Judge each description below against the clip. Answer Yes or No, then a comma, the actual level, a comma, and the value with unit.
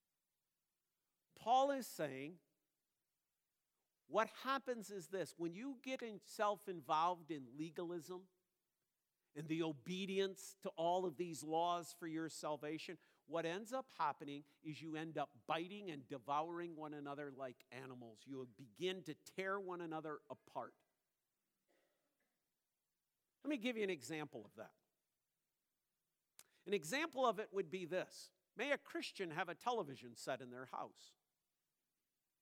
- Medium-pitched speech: Yes, medium, 170 Hz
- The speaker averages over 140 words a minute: No, slow, 135 wpm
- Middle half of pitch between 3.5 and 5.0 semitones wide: Yes, average, 4.5 semitones